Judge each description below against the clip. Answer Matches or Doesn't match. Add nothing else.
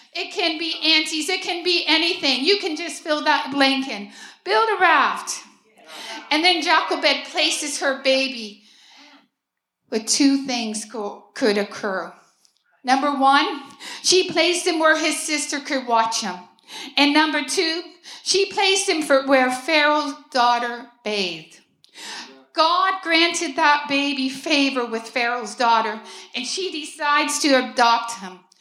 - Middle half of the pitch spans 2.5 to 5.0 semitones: Doesn't match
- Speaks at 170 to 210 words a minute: Doesn't match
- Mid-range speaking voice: Doesn't match